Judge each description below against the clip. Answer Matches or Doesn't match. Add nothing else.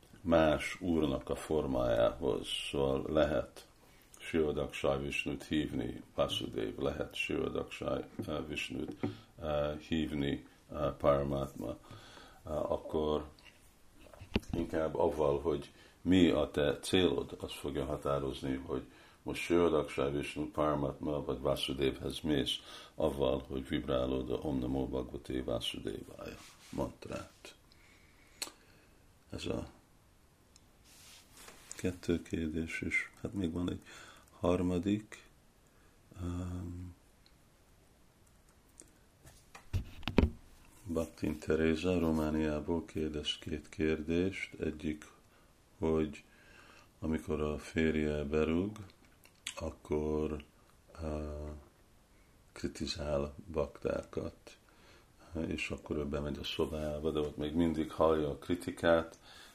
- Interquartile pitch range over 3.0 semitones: Doesn't match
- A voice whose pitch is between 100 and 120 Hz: Doesn't match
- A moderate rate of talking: Doesn't match